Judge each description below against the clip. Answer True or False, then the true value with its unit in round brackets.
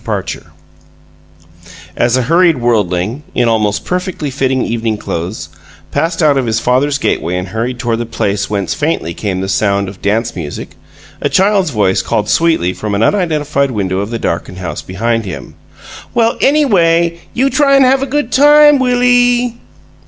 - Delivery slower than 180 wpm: True (165 wpm)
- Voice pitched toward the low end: True (125 Hz)